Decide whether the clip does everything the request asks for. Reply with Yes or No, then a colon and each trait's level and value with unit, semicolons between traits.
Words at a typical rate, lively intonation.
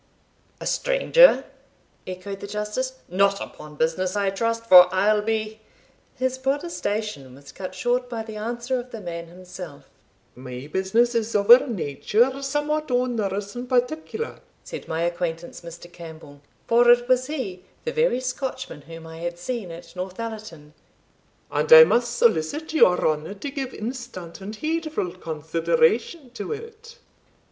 Yes: average, 145 wpm; wide, 6.6 semitones